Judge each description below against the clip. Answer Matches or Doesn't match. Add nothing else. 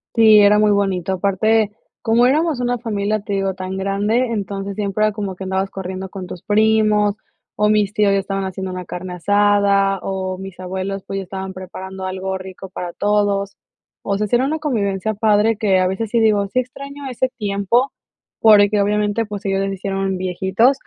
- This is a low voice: Doesn't match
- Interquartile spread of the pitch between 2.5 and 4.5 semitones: Doesn't match